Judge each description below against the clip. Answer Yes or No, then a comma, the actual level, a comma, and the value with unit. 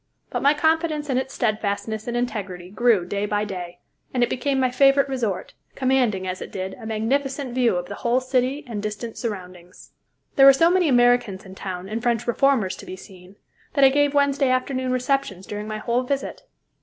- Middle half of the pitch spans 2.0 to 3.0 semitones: No, average, 5.0 semitones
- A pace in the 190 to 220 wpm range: Yes, average, 195 wpm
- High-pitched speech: Yes, high, 240 Hz